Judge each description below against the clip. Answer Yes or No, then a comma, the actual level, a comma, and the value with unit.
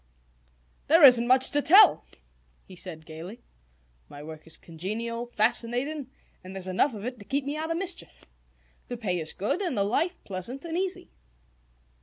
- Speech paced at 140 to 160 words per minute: No, average, 170 wpm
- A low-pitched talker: No, high, 235 Hz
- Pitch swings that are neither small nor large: No, wide, 7.6 semitones